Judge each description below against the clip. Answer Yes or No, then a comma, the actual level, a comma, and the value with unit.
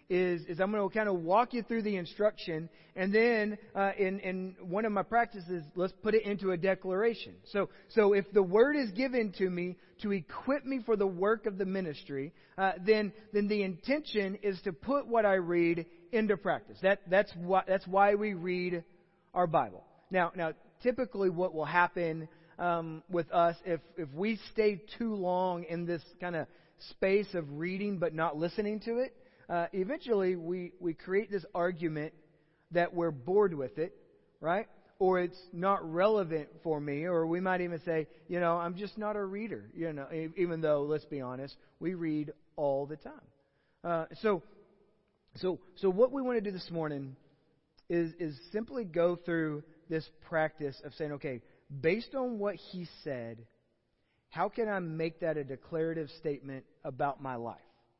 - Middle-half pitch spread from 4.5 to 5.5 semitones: No, average, 4.0 semitones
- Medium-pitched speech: Yes, medium, 180 Hz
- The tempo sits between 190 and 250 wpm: No, average, 180 wpm